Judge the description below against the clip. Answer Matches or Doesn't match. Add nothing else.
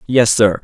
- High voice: Doesn't match